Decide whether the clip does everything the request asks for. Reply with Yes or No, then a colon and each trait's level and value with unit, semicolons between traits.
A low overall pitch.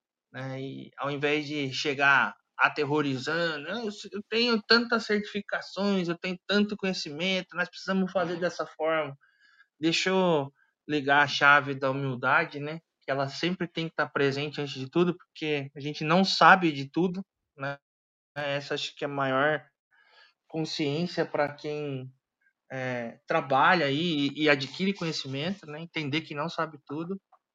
No: medium, 155 Hz